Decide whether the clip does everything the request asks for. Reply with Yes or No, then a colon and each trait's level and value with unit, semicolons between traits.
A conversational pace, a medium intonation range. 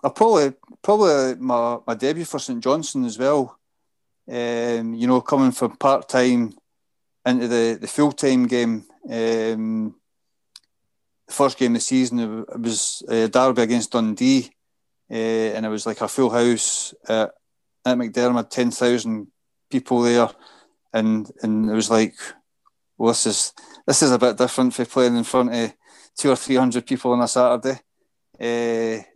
No: average, 165 wpm; narrow, 2.1 semitones